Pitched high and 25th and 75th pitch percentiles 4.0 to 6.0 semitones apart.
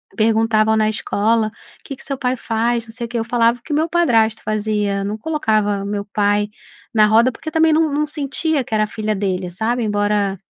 No: high, 220 Hz; average, 3.1 semitones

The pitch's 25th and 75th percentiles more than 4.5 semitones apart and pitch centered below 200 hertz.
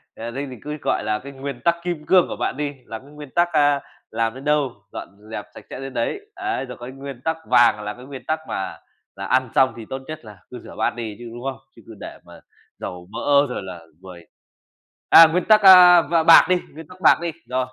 Yes: average, 5.1 semitones; low, 135 Hz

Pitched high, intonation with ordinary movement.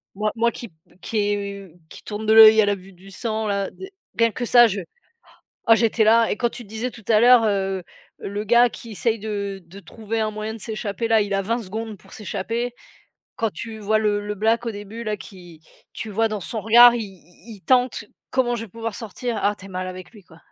No: high, 215 Hz; narrow, 2.3 semitones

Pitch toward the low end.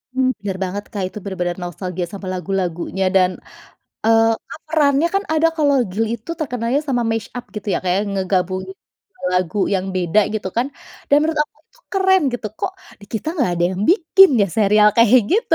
No: high, 215 Hz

